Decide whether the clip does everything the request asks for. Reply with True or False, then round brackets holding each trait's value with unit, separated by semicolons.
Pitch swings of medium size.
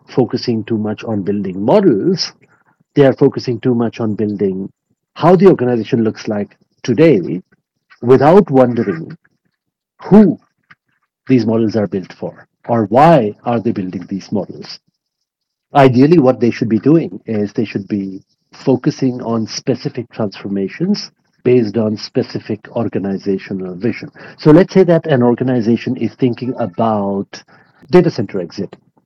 True (3.8 semitones)